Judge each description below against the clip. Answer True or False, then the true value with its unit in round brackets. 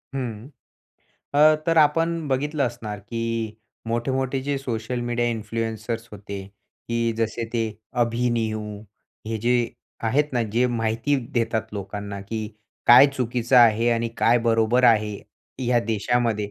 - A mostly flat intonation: True (2.2 semitones)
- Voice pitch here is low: True (115 Hz)